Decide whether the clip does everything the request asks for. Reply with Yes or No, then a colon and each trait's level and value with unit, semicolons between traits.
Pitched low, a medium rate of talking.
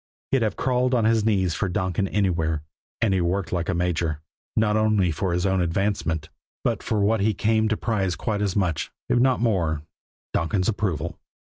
Yes: low, 100 Hz; average, 190 wpm